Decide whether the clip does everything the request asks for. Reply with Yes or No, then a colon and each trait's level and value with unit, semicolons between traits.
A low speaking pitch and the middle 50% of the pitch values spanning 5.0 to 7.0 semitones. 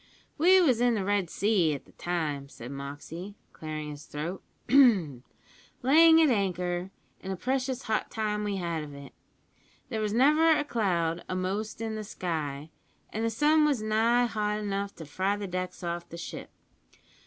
No: high, 200 Hz; average, 5.3 semitones